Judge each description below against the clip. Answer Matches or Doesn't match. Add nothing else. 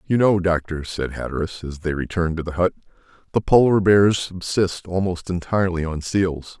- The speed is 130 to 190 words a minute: Matches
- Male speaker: Matches